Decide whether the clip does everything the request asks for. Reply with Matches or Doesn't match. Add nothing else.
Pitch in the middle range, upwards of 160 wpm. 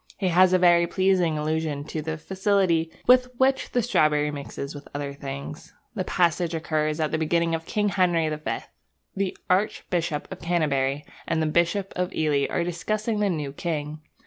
Matches